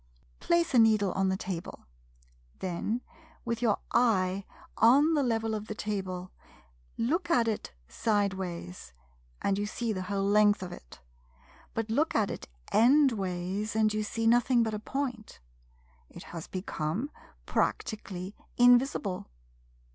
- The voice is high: Yes, high, 215 Hz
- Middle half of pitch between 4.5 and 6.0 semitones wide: No, average, 3.8 semitones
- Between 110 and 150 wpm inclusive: Yes, average, 140 wpm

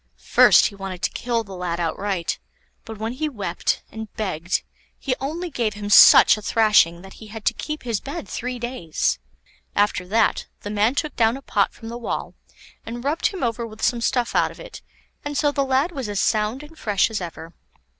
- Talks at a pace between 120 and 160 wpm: No, fast, 205 wpm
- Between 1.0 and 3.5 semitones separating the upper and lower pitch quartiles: No, average, 4.4 semitones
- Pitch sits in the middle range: No, high, 225 Hz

